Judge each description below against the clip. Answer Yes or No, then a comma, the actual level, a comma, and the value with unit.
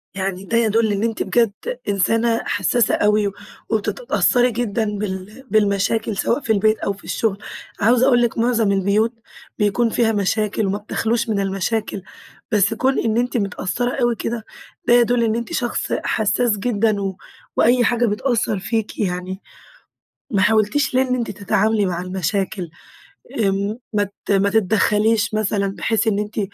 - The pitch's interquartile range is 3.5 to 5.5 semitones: No, narrow, 2.6 semitones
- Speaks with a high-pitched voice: Yes, high, 215 Hz